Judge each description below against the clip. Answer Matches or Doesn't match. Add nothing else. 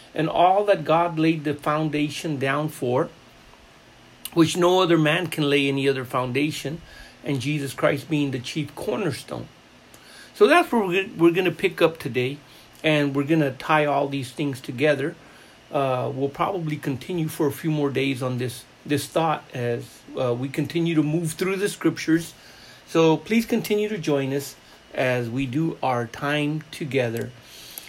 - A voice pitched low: Doesn't match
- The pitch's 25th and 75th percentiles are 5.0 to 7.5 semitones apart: Doesn't match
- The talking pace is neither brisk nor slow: Matches